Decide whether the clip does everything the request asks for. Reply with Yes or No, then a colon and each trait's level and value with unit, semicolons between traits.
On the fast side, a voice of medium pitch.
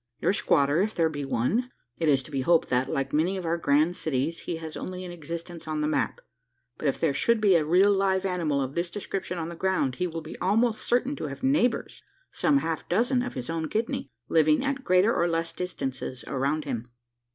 Yes: fast, 220 wpm; medium, 165 Hz